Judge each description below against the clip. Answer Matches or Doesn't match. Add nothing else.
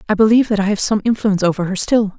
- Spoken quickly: Matches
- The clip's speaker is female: Matches